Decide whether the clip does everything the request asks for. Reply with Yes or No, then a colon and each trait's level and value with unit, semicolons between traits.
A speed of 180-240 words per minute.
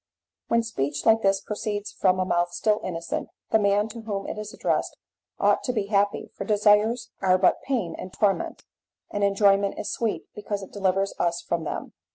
Yes: average, 190 wpm